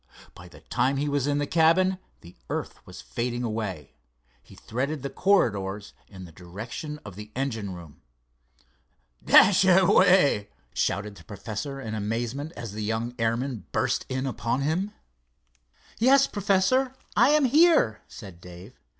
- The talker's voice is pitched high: No, low, 125 Hz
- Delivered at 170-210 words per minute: No, average, 140 wpm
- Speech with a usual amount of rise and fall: No, wide, 8.1 semitones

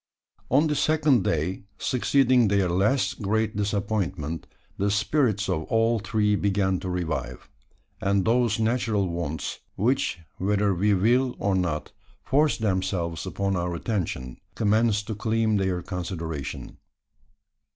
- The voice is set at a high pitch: No, low, 100 Hz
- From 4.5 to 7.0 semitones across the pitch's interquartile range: No, average, 3.8 semitones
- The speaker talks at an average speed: No, slow, 125 wpm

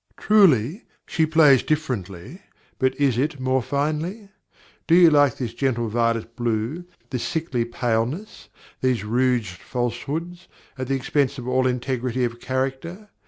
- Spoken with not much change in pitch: No, average, 4.5 semitones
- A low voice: Yes, low, 130 Hz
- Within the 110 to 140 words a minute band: Yes, slow, 135 wpm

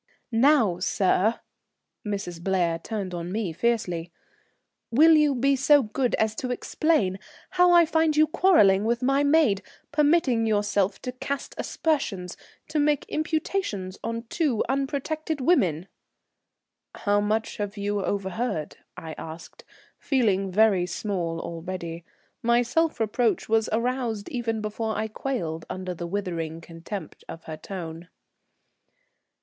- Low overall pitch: No, high, 220 Hz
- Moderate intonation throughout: No, wide, 6.6 semitones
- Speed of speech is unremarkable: No, slow, 130 wpm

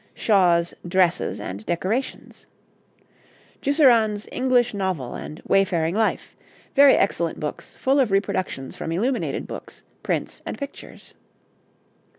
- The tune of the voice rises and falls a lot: Yes, wide, 6.2 semitones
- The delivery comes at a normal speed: No, slow, 110 wpm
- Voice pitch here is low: No, high, 195 Hz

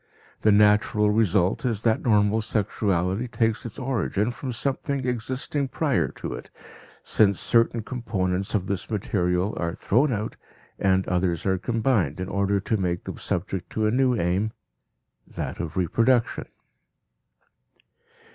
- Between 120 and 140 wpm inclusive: Yes, slow, 135 wpm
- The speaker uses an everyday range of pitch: Yes, average, 3.7 semitones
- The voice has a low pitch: Yes, low, 105 Hz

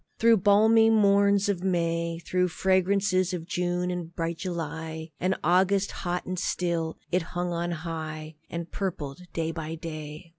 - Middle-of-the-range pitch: Yes, medium, 175 Hz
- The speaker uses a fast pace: No, average, 150 wpm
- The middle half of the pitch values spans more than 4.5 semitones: No, narrow, 2.4 semitones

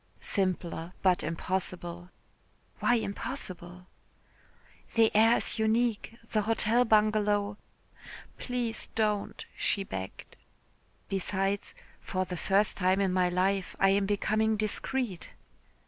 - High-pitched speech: Yes, high, 200 Hz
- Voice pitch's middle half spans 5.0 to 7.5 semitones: No, average, 3.0 semitones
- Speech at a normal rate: No, slow, 105 wpm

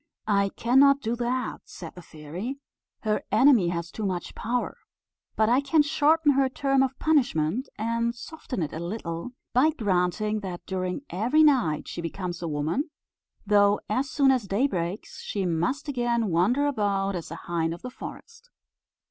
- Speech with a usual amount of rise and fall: No, wide, 7.0 semitones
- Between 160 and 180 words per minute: Yes, average, 165 wpm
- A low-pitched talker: No, high, 220 Hz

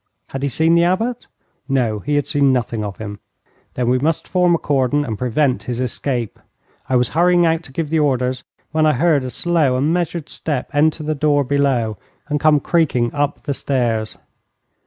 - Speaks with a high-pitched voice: No, medium, 140 Hz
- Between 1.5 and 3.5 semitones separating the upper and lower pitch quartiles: No, average, 4.0 semitones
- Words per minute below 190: No, average, 195 wpm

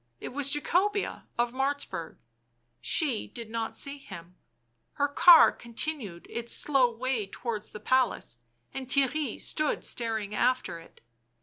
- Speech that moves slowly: Yes, slow, 130 wpm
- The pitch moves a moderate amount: Yes, average, 4.3 semitones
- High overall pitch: Yes, very high, 250 Hz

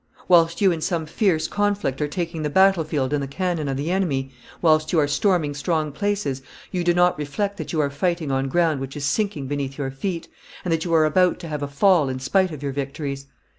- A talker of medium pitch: Yes, medium, 155 Hz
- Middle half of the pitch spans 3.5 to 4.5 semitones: Yes, average, 4.1 semitones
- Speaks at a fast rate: Yes, fast, 235 wpm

